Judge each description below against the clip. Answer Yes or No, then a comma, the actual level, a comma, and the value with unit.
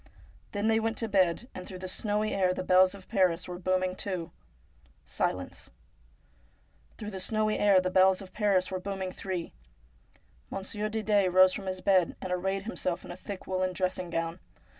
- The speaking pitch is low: No, medium, 185 Hz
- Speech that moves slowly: No, average, 180 wpm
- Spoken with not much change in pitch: Yes, narrow, 1.8 semitones